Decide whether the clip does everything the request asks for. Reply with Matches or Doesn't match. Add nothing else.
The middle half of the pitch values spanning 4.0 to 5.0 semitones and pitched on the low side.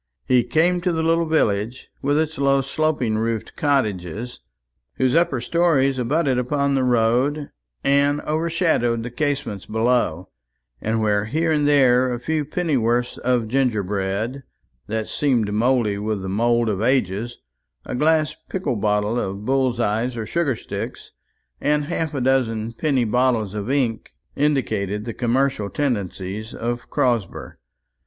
Matches